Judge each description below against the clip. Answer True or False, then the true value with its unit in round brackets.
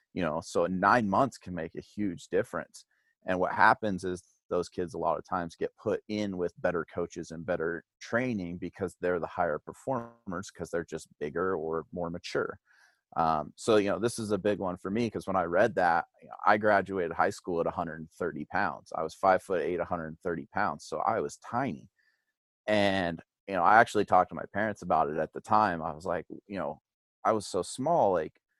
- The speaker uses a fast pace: True (210 wpm)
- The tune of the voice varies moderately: True (3.6 semitones)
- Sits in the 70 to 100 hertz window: True (95 Hz)